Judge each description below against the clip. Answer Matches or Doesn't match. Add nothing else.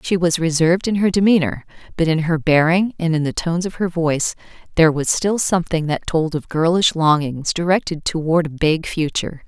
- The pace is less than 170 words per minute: Doesn't match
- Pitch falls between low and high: Matches